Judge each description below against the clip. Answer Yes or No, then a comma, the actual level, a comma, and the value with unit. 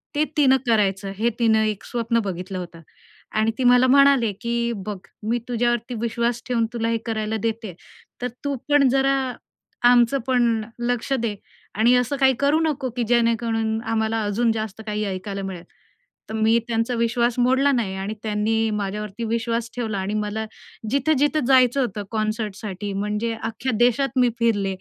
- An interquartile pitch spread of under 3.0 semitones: Yes, narrow, 2.4 semitones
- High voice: Yes, high, 230 Hz